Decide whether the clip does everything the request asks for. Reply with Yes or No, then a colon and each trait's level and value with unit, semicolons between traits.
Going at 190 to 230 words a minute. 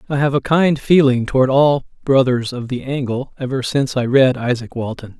Yes: average, 195 wpm